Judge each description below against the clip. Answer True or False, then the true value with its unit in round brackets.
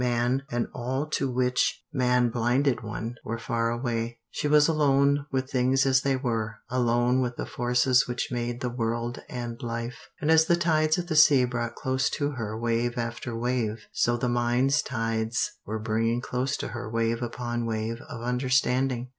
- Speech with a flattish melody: True (1.9 semitones)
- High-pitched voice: False (120 Hz)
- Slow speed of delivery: False (180 wpm)